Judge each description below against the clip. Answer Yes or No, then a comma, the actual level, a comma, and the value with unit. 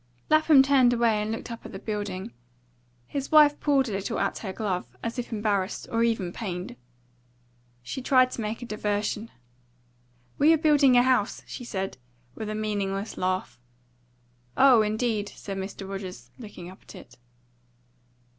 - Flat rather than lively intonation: No, average, 4.3 semitones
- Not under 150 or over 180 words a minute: Yes, average, 160 wpm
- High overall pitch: Yes, high, 215 Hz